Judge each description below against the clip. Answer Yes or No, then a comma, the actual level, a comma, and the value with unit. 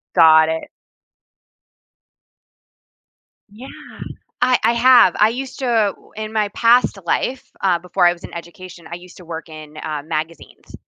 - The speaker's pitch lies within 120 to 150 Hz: No, medium, 180 Hz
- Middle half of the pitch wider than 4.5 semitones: Yes, wide, 5.6 semitones